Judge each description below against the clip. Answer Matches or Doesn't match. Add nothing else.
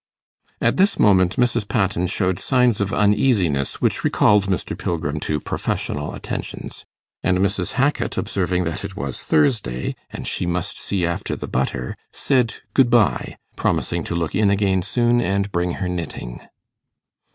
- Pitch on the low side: Matches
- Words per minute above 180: Doesn't match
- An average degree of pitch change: Matches